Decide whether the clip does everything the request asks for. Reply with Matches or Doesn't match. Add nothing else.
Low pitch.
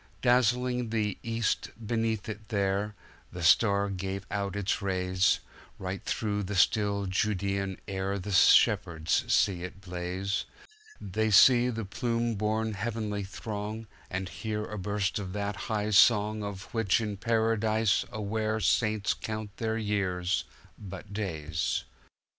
Matches